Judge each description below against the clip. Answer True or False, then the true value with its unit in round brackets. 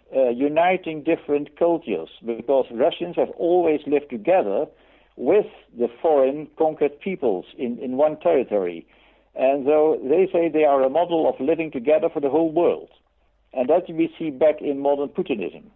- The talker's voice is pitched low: False (155 Hz)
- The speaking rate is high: False (160 wpm)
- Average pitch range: True (3.3 semitones)